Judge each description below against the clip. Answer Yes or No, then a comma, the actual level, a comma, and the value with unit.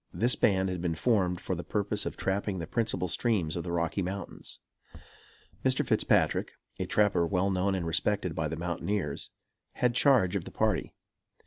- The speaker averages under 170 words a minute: No, average, 175 wpm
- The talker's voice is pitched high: No, very low, 95 Hz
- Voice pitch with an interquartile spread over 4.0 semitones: No, average, 3.2 semitones